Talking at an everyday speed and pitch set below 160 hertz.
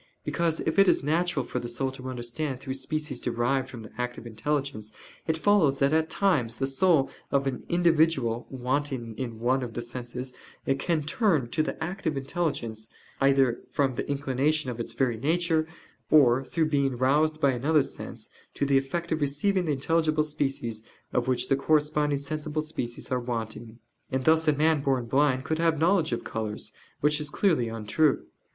Yes: average, 180 wpm; medium, 140 Hz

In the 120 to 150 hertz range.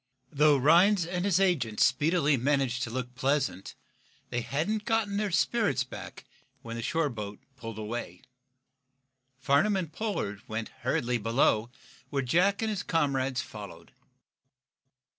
Yes: medium, 140 Hz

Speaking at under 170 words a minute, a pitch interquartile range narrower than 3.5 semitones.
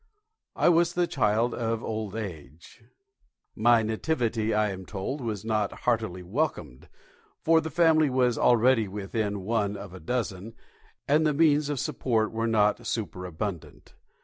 No: average, 145 wpm; average, 4.2 semitones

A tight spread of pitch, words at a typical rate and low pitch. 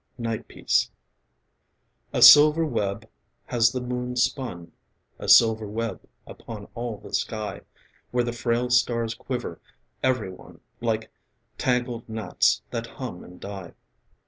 No: narrow, 2.3 semitones; slow, 125 wpm; low, 115 Hz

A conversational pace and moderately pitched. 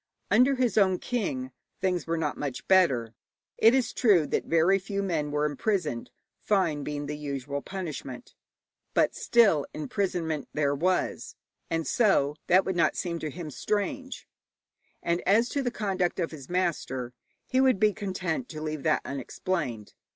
Yes: average, 160 wpm; medium, 170 Hz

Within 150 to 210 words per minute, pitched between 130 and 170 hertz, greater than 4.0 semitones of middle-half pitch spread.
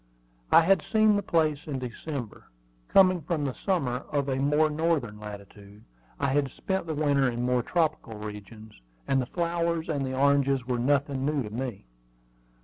Yes: average, 170 wpm; medium, 140 Hz; average, 4.6 semitones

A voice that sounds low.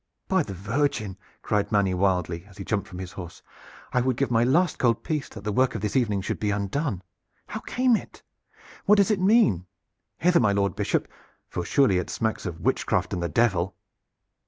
Yes: low, 105 Hz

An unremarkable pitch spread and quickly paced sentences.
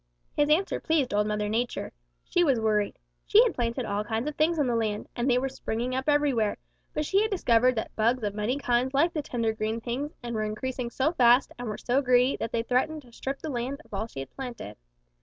Yes: average, 4.0 semitones; fast, 240 wpm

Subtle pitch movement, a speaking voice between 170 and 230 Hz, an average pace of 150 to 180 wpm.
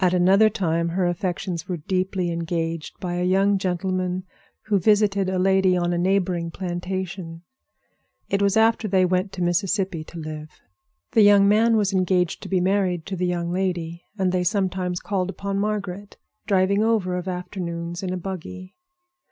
Yes: narrow, 1.9 semitones; medium, 185 Hz; average, 170 wpm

